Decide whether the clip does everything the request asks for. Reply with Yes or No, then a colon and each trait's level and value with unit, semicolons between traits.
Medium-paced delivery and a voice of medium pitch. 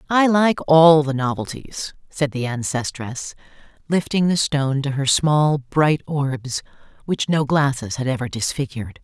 Yes: average, 145 wpm; medium, 145 Hz